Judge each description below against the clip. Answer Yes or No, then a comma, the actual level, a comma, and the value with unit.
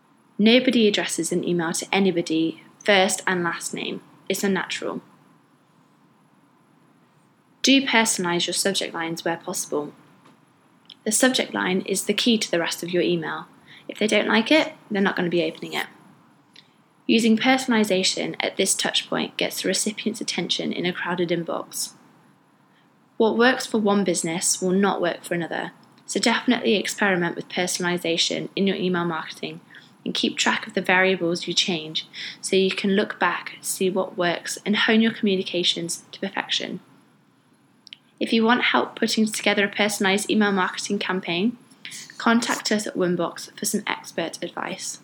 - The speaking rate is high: No, average, 155 wpm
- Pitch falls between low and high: No, high, 195 Hz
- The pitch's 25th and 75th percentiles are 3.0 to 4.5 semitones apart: Yes, average, 4.0 semitones